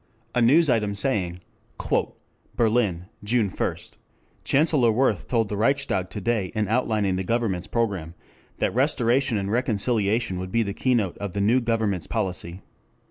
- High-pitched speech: No, low, 110 Hz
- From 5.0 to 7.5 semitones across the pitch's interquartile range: No, average, 3.8 semitones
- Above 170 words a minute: No, average, 150 wpm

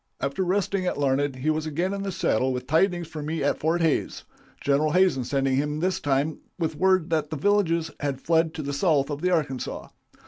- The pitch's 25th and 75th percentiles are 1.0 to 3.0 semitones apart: No, average, 3.7 semitones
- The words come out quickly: Yes, fast, 210 wpm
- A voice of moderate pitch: Yes, medium, 155 Hz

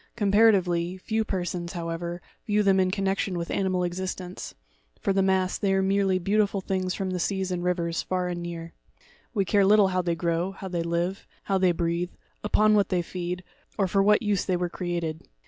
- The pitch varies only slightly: Yes, narrow, 2.0 semitones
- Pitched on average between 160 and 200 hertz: Yes, medium, 185 Hz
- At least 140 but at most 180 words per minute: No, average, 195 wpm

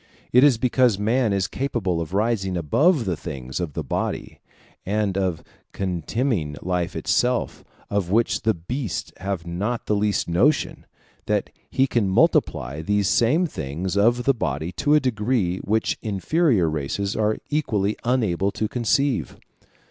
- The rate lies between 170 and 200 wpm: No, average, 150 wpm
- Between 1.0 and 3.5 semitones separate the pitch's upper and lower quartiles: No, wide, 5.5 semitones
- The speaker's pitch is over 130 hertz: No, low, 105 Hz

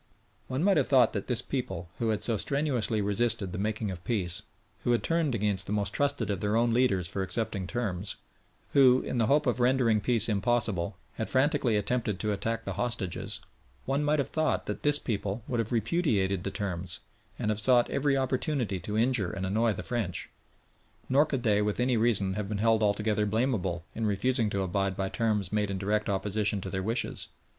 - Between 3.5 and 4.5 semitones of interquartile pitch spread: Yes, average, 3.9 semitones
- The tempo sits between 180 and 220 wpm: Yes, average, 200 wpm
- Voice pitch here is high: No, low, 110 Hz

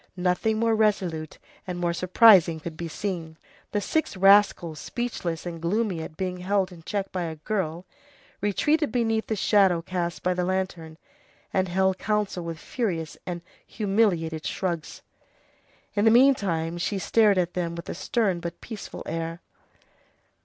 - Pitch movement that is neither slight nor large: Yes, average, 3.6 semitones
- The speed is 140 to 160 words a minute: Yes, average, 155 wpm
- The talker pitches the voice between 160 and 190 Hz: Yes, medium, 185 Hz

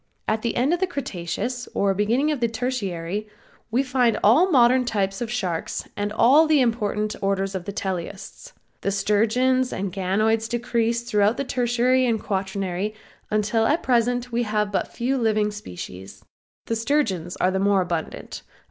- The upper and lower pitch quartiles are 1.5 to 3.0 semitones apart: No, average, 3.9 semitones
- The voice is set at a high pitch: Yes, high, 220 Hz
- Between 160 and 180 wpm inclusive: Yes, average, 170 wpm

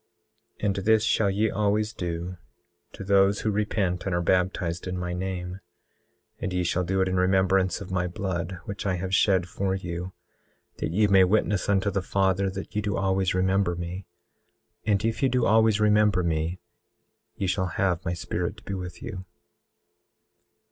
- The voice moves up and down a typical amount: No, narrow, 1.9 semitones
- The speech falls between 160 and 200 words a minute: Yes, average, 180 wpm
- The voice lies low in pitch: Yes, very low, 95 Hz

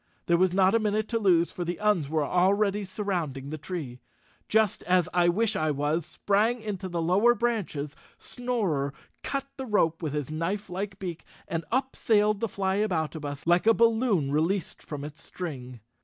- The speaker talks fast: No, average, 170 wpm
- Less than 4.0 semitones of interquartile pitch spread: No, average, 5.0 semitones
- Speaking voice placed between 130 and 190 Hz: Yes, medium, 185 Hz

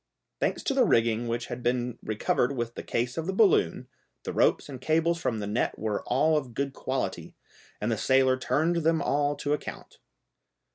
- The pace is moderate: Yes, average, 190 wpm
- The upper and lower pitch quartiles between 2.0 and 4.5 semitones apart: No, average, 4.9 semitones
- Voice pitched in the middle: No, low, 130 Hz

